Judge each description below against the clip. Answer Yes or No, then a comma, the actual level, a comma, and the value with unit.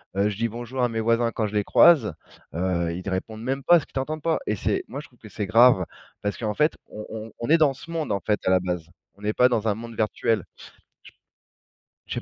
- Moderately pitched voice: No, low, 110 Hz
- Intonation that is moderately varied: Yes, average, 3.7 semitones